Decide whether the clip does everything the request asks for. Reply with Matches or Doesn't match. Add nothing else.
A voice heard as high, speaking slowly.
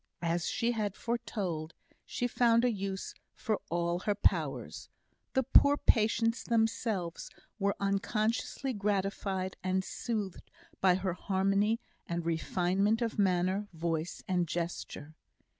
Matches